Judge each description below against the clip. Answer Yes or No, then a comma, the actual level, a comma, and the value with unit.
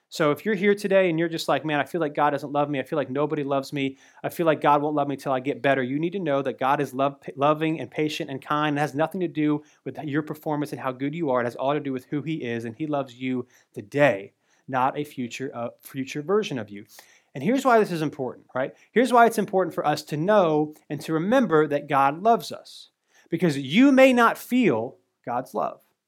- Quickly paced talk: Yes, fast, 255 wpm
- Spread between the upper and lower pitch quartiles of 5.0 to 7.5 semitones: No, average, 3.3 semitones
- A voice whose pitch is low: No, medium, 150 Hz